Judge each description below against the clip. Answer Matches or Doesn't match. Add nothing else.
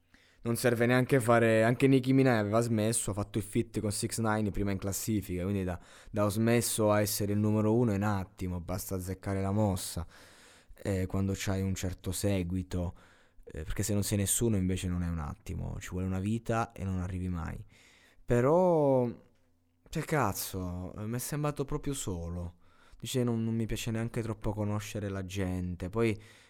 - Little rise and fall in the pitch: Doesn't match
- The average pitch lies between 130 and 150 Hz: Doesn't match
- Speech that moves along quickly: Matches